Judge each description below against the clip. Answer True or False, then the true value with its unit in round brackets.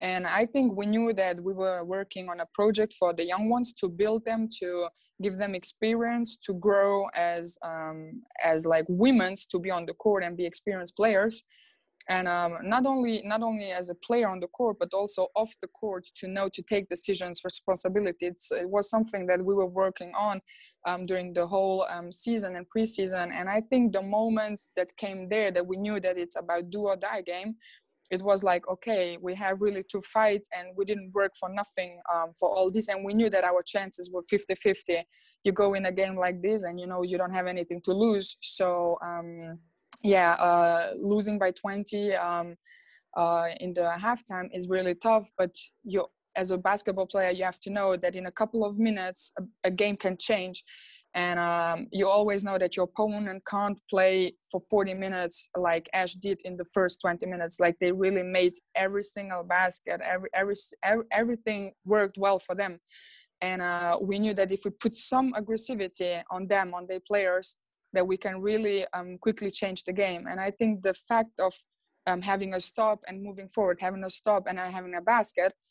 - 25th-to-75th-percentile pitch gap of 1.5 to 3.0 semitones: True (2.4 semitones)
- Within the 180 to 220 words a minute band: True (205 wpm)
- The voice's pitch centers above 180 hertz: True (190 Hz)